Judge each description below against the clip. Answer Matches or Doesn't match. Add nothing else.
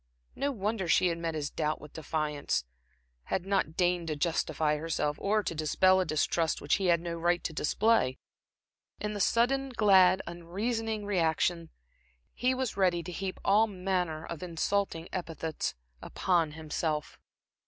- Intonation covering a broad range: Doesn't match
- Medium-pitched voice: Matches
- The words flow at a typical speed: Matches